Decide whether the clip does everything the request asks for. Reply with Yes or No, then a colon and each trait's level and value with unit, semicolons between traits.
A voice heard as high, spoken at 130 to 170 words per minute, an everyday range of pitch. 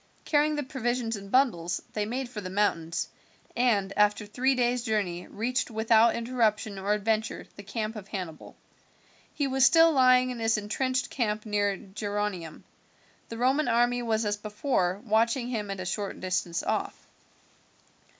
Yes: high, 220 Hz; average, 155 wpm; average, 3.5 semitones